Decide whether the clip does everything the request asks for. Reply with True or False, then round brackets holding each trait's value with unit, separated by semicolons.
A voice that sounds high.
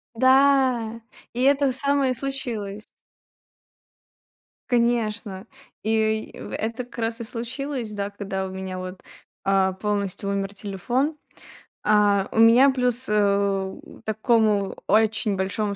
True (220 Hz)